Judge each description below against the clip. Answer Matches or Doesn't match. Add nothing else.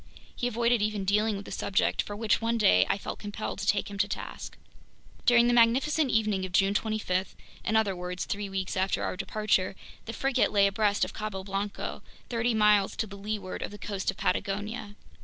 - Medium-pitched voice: Doesn't match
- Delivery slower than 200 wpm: Matches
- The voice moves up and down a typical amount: Doesn't match